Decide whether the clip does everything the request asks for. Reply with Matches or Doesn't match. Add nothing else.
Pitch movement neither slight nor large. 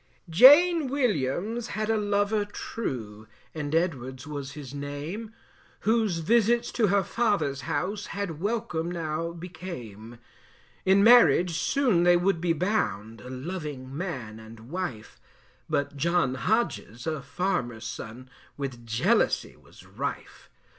Doesn't match